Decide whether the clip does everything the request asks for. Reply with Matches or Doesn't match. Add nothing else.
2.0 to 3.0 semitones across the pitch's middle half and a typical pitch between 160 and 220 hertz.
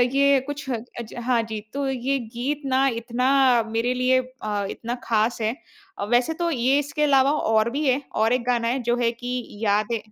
Doesn't match